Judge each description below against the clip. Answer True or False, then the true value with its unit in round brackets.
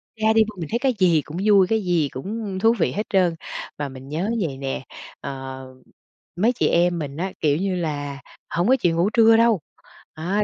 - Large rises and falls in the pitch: True (6.3 semitones)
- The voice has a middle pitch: True (175 Hz)